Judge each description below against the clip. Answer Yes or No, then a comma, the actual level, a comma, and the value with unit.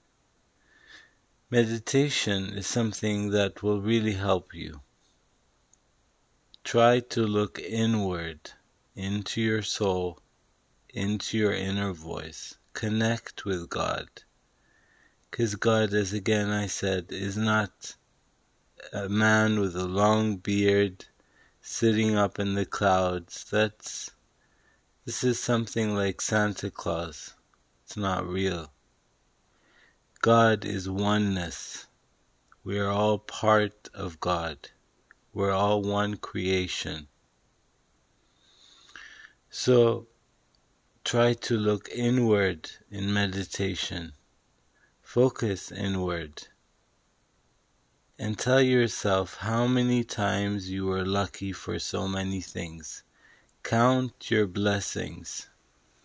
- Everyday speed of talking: No, slow, 95 wpm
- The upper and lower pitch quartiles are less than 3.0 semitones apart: Yes, narrow, 2.6 semitones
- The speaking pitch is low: Yes, low, 100 Hz